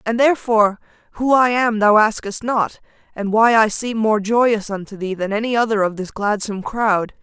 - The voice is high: Yes, high, 215 Hz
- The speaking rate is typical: Yes, average, 190 wpm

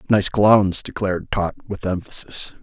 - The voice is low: Yes, very low, 95 Hz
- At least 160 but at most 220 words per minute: No, slow, 135 wpm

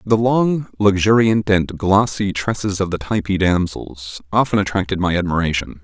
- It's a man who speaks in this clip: Yes, male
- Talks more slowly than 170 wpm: Yes, average, 145 wpm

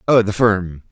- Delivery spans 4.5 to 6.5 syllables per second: No, 4.3 syllables/s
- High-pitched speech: No, low, 100 Hz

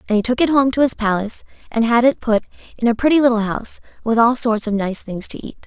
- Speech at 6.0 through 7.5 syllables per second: Yes, 6.5 syllables/s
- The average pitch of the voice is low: No, high, 230 Hz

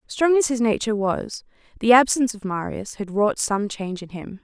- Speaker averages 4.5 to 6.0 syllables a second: Yes, 5.3 syllables/s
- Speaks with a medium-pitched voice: No, high, 220 Hz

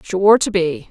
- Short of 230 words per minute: Yes, average, 200 wpm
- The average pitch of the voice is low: No, medium, 180 Hz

